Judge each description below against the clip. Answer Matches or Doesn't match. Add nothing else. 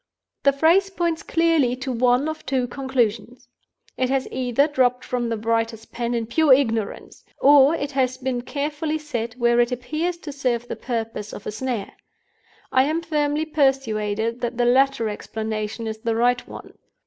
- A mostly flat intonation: Doesn't match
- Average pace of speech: Matches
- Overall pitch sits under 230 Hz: Doesn't match